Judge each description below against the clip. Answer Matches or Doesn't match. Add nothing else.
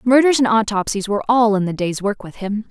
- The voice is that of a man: Doesn't match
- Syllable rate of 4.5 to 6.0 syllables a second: Matches